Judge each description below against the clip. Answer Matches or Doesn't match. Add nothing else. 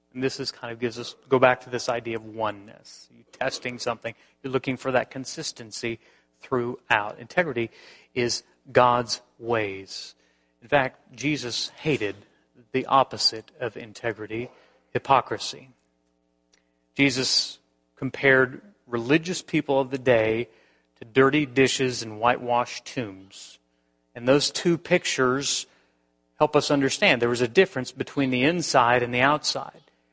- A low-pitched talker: Matches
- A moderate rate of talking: Doesn't match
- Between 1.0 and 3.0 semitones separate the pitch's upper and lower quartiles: Doesn't match